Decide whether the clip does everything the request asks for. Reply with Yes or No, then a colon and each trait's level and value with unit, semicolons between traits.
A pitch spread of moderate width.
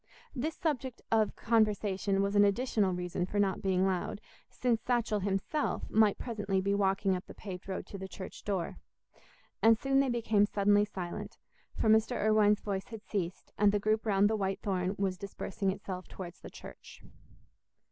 No: narrow, 2.3 semitones